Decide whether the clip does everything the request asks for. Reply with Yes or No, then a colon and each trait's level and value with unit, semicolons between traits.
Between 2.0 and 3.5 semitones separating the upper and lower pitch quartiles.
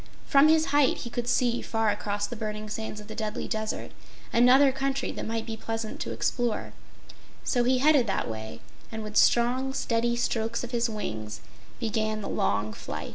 Yes: narrow, 2.6 semitones